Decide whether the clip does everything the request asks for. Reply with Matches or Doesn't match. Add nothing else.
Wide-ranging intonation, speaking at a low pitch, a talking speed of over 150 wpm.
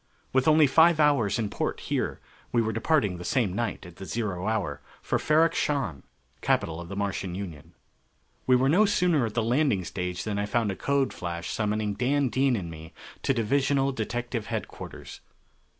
Matches